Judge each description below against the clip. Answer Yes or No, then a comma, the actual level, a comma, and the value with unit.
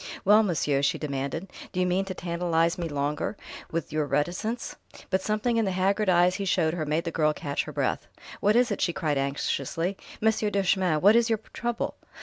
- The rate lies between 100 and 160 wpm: No, average, 200 wpm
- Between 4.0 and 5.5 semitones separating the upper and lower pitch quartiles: Yes, average, 4.5 semitones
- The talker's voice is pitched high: No, medium, 180 Hz